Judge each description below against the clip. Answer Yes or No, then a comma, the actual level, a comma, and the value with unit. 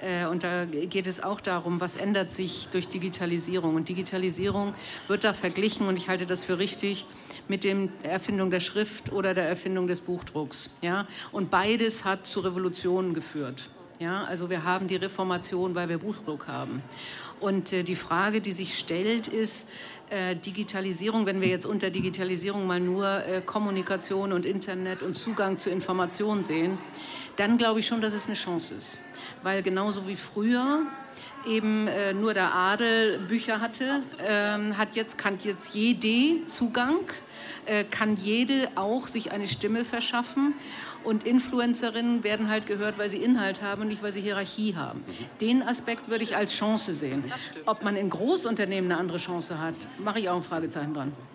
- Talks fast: No, average, 170 wpm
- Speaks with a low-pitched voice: No, high, 195 Hz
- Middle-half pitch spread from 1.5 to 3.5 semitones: Yes, average, 3.1 semitones